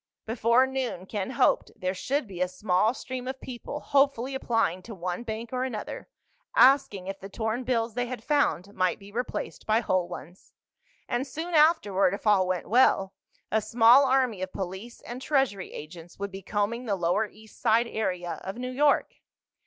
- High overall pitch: Yes, high, 220 Hz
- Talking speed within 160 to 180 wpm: Yes, average, 175 wpm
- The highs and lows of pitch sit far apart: No, average, 5.0 semitones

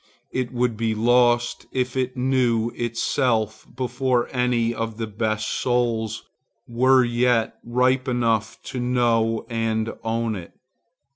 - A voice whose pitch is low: Yes, low, 120 Hz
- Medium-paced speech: No, slow, 125 wpm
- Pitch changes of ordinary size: No, narrow, 1.7 semitones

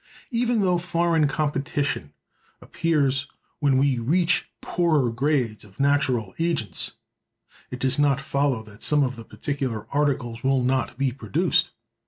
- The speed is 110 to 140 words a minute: Yes, slow, 135 wpm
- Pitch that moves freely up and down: No, average, 3.7 semitones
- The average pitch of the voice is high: No, medium, 140 Hz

